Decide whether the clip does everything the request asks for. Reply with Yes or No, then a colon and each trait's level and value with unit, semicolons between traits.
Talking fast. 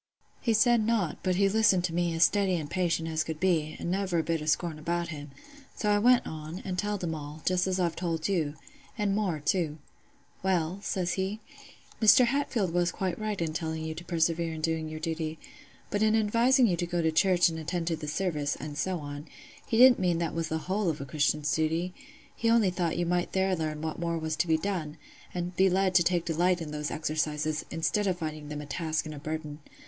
Yes: fast, 225 wpm